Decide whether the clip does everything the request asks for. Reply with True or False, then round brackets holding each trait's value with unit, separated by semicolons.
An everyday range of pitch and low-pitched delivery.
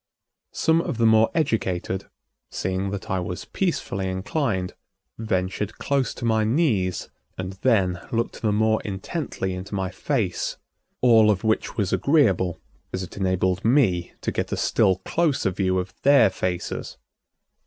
True (3.9 semitones; 100 Hz)